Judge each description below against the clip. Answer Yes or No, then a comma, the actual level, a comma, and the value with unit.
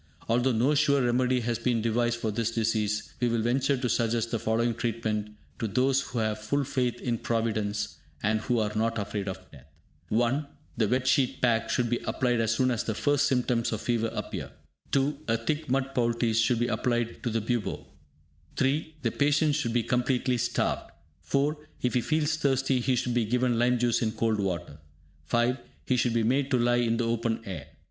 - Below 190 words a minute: No, average, 200 wpm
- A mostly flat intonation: Yes, narrow, 2.2 semitones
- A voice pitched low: Yes, low, 120 Hz